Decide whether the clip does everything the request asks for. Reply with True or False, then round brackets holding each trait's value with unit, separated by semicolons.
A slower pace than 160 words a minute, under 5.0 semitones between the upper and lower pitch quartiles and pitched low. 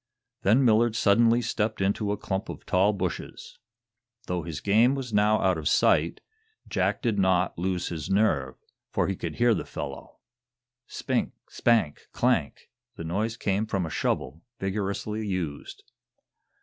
True (150 wpm; 3.6 semitones; 100 Hz)